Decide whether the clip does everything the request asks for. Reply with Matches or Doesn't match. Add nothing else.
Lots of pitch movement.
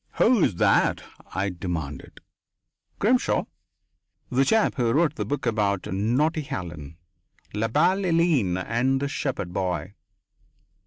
Matches